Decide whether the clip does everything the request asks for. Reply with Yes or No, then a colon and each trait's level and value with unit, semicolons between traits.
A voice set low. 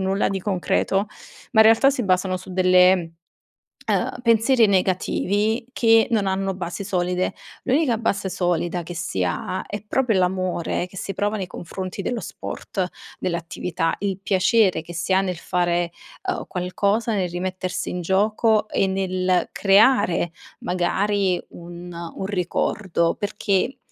No: high, 190 Hz